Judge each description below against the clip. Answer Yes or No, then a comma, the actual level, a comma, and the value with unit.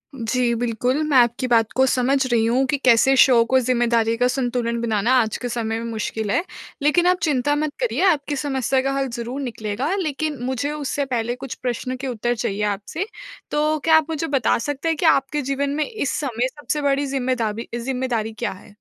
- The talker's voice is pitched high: Yes, very high, 255 Hz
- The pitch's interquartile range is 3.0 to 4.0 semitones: Yes, average, 3.6 semitones